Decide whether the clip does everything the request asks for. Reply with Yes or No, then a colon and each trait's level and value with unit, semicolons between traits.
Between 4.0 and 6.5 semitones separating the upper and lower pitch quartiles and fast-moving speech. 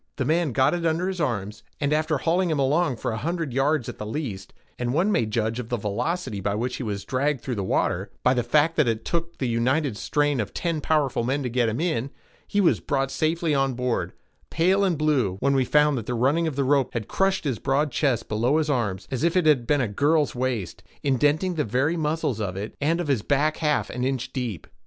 Yes: average, 4.8 semitones; fast, 235 wpm